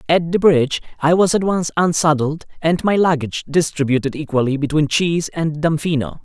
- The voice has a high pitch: No, medium, 155 Hz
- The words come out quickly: No, average, 165 wpm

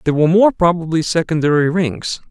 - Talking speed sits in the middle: Yes, average, 155 wpm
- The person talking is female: No, male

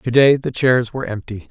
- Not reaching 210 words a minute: Yes, average, 200 wpm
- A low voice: Yes, low, 125 Hz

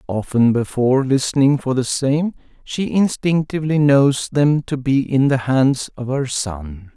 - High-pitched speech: No, low, 135 Hz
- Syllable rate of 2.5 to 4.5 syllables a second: Yes, 4.2 syllables/s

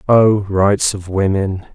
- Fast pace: No, average, 140 wpm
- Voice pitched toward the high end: No, low, 100 Hz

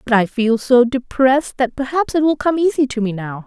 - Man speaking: No, female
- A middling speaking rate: No, fast, 240 wpm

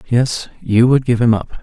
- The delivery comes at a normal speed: No, fast, 220 wpm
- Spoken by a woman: No, male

